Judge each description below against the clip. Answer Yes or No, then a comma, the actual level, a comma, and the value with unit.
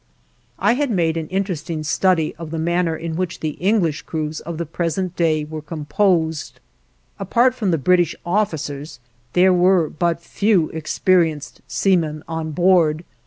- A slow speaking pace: No, average, 150 wpm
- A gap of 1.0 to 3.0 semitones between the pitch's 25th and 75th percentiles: Yes, average, 2.7 semitones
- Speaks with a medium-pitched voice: Yes, medium, 165 Hz